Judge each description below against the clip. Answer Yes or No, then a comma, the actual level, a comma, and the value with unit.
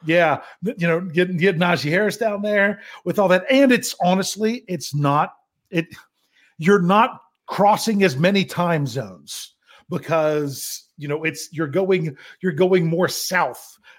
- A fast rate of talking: No, average, 150 wpm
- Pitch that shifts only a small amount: No, average, 3.5 semitones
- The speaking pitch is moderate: Yes, medium, 180 Hz